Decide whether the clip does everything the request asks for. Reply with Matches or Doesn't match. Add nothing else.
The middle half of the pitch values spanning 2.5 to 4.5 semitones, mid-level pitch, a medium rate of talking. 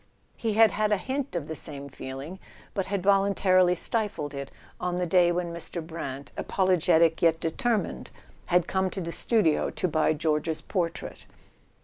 Matches